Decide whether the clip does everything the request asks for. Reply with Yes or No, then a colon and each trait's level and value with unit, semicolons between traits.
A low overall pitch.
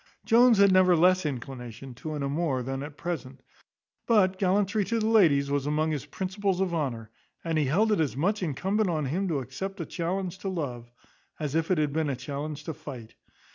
No: medium, 160 Hz